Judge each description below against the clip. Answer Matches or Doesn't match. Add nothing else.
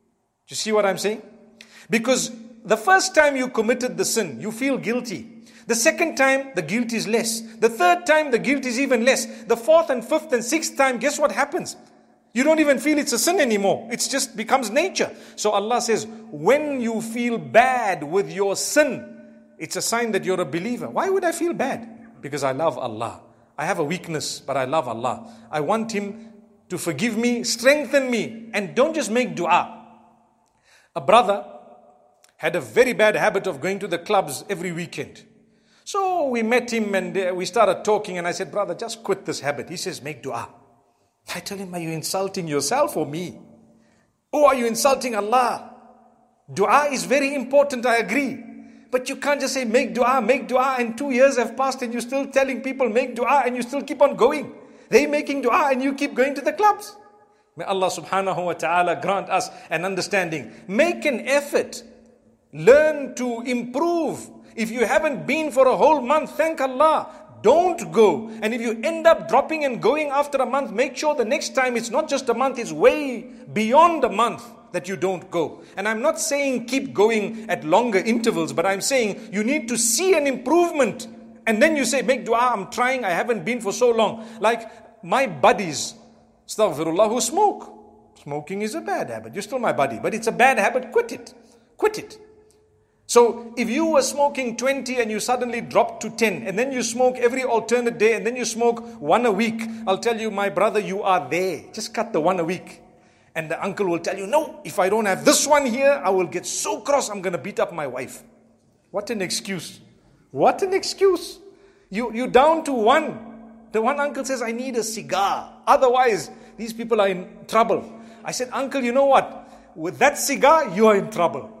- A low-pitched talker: Doesn't match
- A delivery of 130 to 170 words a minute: Doesn't match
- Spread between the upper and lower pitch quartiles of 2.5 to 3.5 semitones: Doesn't match